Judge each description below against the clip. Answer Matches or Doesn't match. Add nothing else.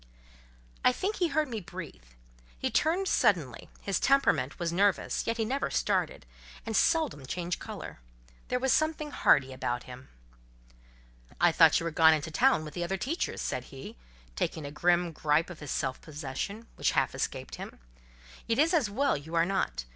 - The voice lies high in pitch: Doesn't match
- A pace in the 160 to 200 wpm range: Matches